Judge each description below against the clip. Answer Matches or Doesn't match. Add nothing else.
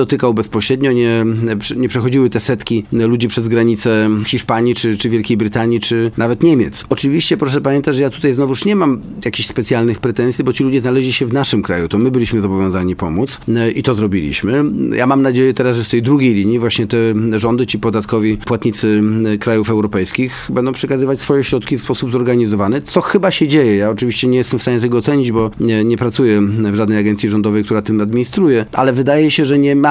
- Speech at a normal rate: Doesn't match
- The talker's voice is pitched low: Matches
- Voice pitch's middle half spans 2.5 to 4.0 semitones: Matches